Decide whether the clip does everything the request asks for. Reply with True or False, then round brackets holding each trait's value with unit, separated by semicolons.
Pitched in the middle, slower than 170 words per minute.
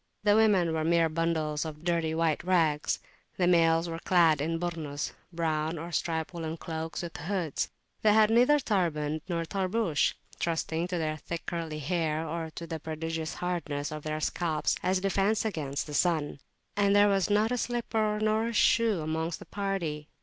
False (165 Hz; 180 wpm)